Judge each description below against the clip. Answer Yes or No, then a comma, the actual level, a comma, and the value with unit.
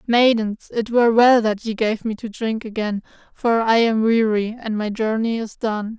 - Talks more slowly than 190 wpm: No, average, 200 wpm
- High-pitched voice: Yes, high, 225 Hz